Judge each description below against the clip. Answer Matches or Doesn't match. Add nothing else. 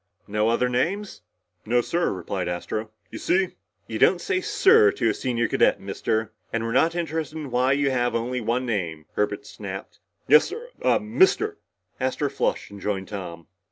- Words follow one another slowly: Doesn't match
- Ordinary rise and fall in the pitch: Doesn't match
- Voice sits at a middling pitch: Doesn't match